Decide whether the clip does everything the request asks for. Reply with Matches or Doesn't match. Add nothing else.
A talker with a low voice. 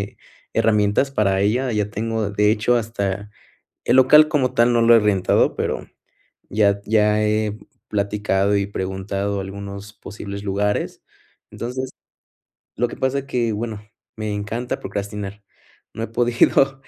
Matches